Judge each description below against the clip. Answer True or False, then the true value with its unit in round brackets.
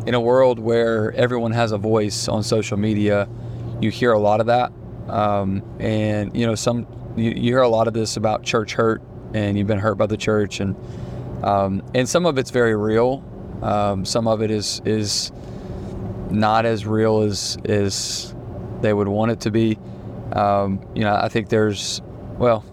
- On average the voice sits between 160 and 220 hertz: False (110 Hz)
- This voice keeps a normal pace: True (185 wpm)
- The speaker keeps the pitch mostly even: True (2.1 semitones)